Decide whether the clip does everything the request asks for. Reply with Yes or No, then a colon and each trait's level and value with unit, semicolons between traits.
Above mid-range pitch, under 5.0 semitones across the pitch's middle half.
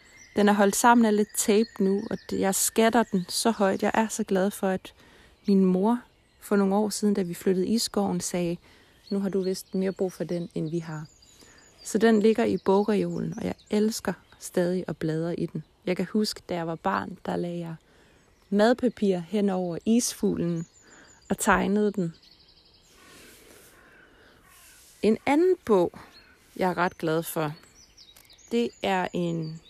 Yes: high, 195 Hz; average, 3.3 semitones